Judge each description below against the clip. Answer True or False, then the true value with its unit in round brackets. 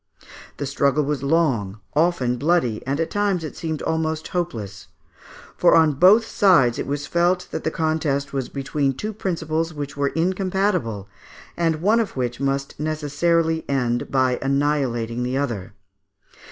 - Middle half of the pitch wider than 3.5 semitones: True (4.0 semitones)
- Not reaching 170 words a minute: True (150 wpm)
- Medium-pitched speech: True (150 Hz)